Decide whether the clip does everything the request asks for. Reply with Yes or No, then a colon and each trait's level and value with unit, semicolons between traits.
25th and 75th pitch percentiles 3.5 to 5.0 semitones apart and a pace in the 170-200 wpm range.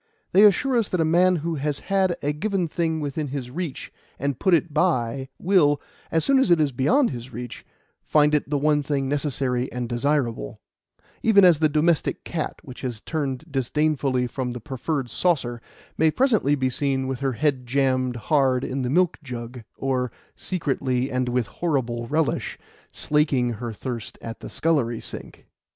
Yes: average, 4.1 semitones; average, 175 wpm